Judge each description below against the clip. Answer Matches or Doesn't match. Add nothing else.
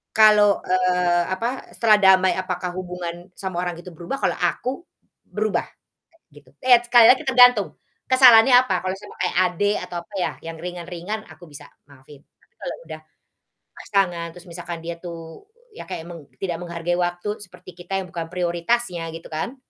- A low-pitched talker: Doesn't match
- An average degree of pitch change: Matches